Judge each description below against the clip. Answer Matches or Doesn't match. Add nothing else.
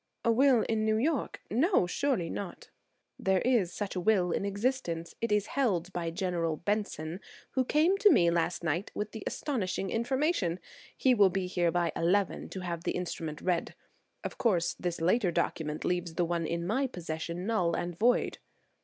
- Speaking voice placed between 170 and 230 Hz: Matches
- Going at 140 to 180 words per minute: Matches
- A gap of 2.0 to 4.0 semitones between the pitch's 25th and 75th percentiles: Doesn't match